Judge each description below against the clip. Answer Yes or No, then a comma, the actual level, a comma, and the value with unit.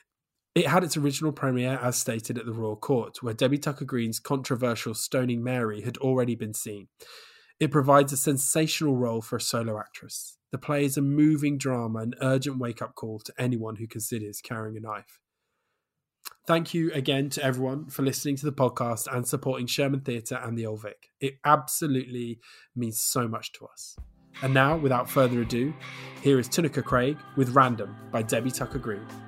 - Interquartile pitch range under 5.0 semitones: Yes, average, 3.2 semitones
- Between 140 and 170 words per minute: No, average, 180 wpm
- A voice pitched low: Yes, low, 130 Hz